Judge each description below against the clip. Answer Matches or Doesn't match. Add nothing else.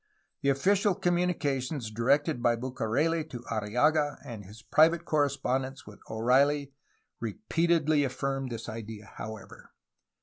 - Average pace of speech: Doesn't match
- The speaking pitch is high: Doesn't match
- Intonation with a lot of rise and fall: Doesn't match